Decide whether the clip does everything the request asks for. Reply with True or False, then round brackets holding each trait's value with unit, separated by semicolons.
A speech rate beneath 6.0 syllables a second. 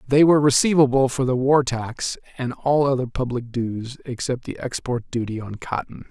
True (5.0 syllables/s)